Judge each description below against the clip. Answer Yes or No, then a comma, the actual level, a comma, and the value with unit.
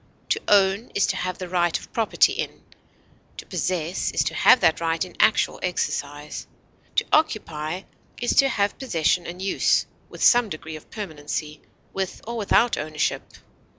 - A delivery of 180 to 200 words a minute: No, average, 160 wpm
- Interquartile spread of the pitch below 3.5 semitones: No, average, 4.6 semitones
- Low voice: No, medium, 185 Hz